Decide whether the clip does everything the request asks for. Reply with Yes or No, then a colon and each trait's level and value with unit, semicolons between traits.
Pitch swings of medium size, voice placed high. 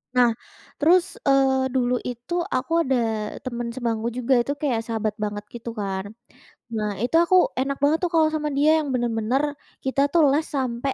Yes: average, 3.5 semitones; very high, 255 Hz